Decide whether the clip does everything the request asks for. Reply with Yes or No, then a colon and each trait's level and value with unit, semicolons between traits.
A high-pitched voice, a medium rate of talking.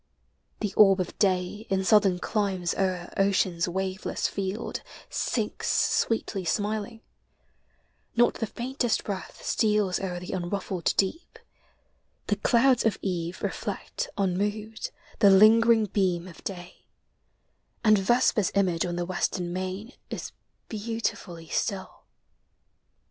No: high, 195 Hz; slow, 115 wpm